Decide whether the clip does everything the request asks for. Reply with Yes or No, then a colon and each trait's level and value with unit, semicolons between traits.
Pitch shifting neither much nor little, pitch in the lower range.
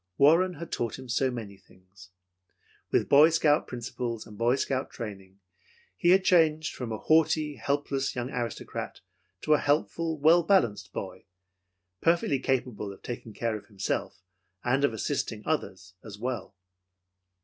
No: wide, 6.0 semitones; low, 130 Hz